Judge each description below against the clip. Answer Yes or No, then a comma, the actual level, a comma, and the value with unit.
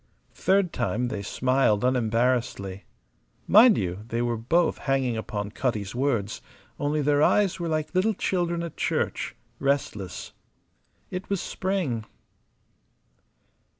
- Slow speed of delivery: Yes, slow, 115 wpm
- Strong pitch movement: Yes, wide, 7.3 semitones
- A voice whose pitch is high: No, low, 130 Hz